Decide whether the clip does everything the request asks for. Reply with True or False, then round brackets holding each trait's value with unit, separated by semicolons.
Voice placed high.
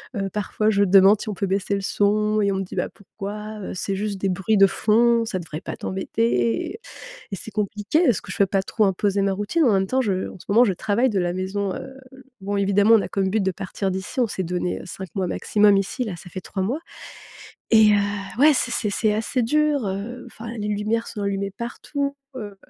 True (205 Hz)